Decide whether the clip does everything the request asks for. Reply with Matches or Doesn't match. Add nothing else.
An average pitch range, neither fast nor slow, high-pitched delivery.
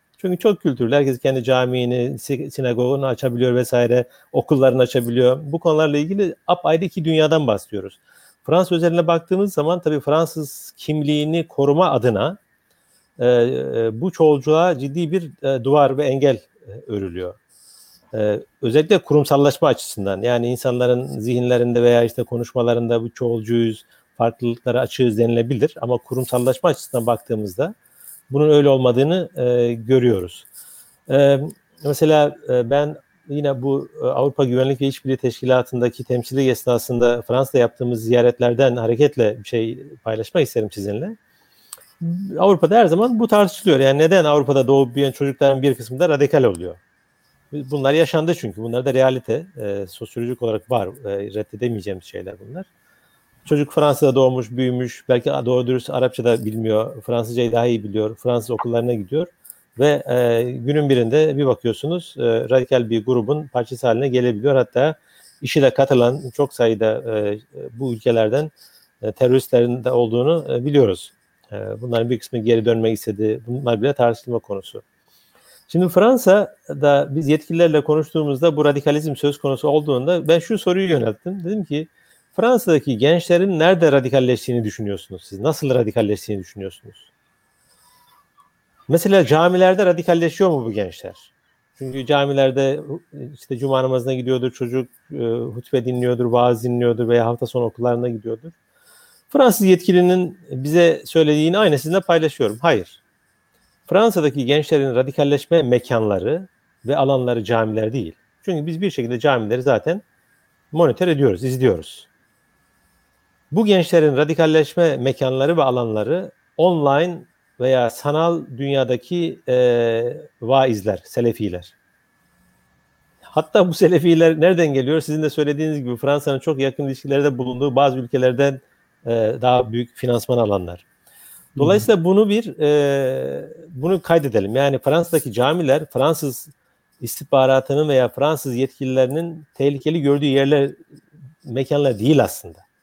Doesn't match